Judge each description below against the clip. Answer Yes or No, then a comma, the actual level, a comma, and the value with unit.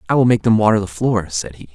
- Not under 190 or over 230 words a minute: No, fast, 310 wpm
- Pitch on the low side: Yes, low, 100 Hz